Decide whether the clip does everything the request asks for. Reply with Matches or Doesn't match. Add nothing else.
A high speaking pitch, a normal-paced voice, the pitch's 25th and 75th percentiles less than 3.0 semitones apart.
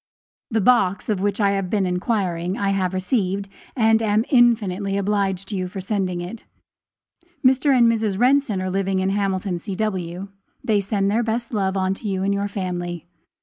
Matches